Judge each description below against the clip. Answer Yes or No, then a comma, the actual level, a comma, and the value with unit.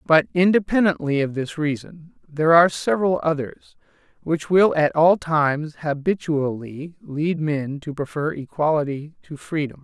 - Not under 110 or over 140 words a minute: Yes, slow, 135 wpm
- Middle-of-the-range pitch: Yes, medium, 155 Hz